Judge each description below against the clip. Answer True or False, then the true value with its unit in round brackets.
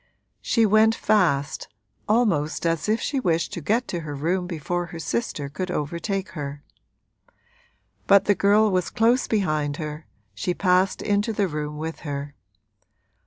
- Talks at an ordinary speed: True (150 wpm)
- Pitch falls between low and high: True (175 Hz)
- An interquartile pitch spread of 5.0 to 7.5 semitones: True (5.4 semitones)